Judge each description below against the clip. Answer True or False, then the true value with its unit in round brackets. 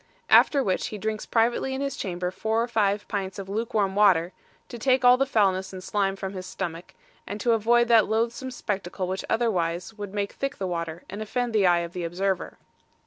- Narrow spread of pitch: False (3.7 semitones)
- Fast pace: True (210 wpm)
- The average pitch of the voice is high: True (205 Hz)